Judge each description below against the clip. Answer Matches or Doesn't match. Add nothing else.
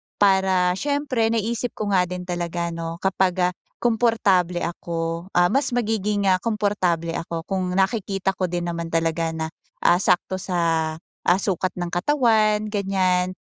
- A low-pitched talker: Doesn't match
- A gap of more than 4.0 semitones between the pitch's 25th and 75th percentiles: Doesn't match